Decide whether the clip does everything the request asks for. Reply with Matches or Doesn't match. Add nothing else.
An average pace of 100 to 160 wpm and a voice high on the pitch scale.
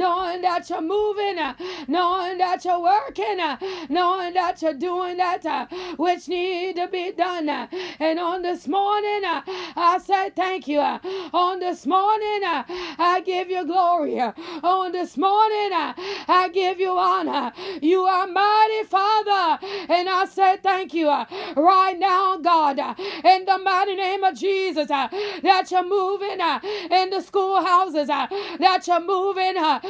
Matches